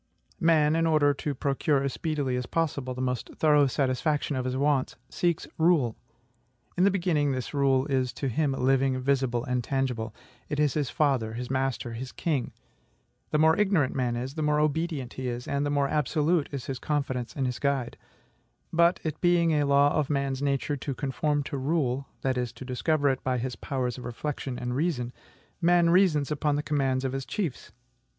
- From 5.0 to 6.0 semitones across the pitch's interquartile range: No, average, 2.9 semitones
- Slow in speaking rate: No, average, 190 wpm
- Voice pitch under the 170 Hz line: Yes, medium, 140 Hz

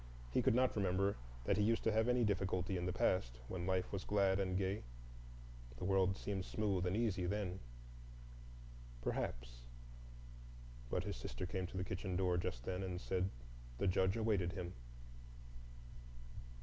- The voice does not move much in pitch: Yes, narrow, 2.0 semitones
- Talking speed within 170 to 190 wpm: No, average, 155 wpm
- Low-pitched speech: Yes, very low, 95 Hz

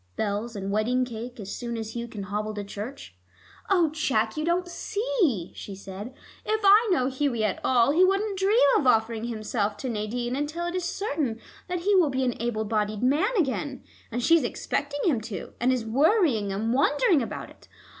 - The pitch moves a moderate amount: No, wide, 7.0 semitones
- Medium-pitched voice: No, very high, 250 Hz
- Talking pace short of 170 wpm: No, average, 195 wpm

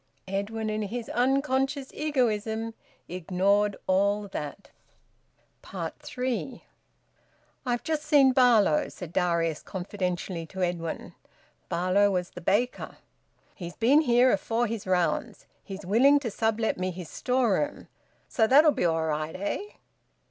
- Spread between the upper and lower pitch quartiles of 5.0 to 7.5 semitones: Yes, wide, 5.4 semitones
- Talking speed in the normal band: No, slow, 120 wpm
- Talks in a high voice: Yes, high, 210 Hz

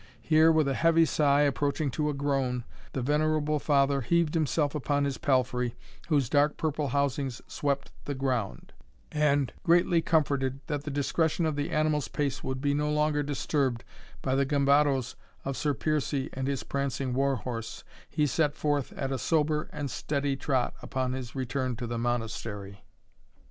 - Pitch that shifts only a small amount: Yes, narrow, 2.2 semitones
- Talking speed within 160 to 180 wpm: Yes, average, 165 wpm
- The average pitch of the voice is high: No, medium, 140 Hz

